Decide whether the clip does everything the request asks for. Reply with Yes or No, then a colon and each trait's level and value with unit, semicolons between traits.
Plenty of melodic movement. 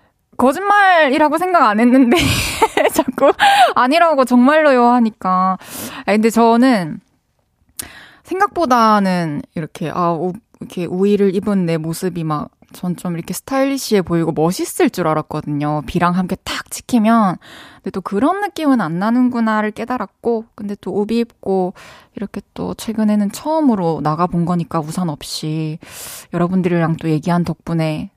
Yes: wide, 6.6 semitones